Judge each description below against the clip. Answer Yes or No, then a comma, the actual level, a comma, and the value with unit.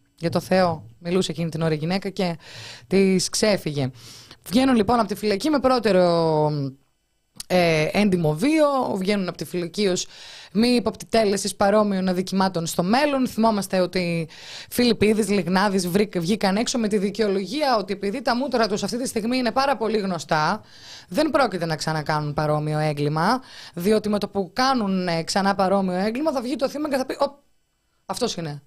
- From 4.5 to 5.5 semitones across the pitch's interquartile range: Yes, average, 5.1 semitones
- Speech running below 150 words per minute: No, average, 165 wpm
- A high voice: Yes, high, 195 Hz